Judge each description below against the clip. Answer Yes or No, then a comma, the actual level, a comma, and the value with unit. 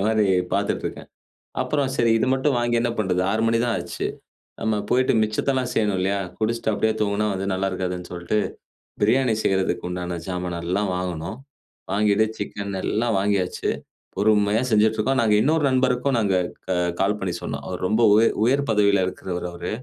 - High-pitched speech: No, low, 105 Hz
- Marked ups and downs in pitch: No, average, 3.6 semitones